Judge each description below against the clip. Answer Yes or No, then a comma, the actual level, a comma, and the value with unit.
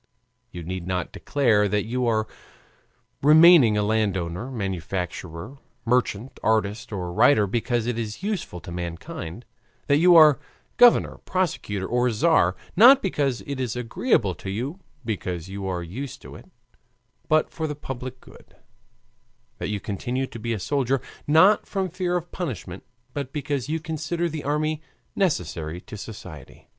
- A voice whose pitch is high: No, low, 120 Hz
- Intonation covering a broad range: Yes, wide, 7.3 semitones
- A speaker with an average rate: Yes, average, 150 wpm